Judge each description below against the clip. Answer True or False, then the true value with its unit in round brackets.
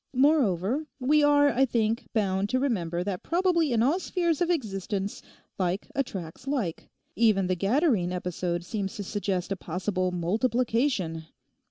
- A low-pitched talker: False (215 Hz)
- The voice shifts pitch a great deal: True (6.9 semitones)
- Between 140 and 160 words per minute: True (145 wpm)